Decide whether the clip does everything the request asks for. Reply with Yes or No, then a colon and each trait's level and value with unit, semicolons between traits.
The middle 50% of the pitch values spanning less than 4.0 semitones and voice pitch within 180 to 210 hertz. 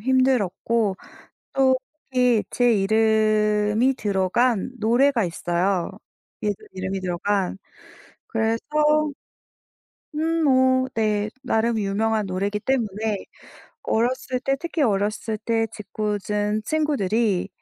No: average, 3.6 semitones; high, 220 Hz